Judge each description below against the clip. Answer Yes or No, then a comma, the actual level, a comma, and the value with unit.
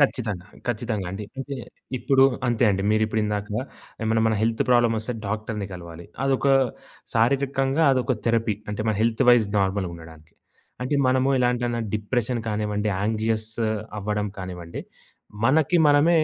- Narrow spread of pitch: No, average, 3.3 semitones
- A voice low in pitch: Yes, low, 110 Hz